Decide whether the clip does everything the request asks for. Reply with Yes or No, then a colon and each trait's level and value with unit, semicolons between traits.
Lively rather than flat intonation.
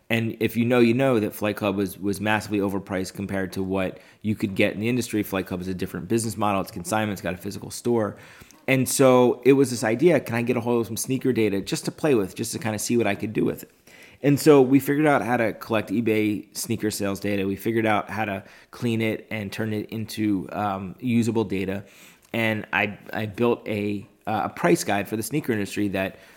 No: average, 2.7 semitones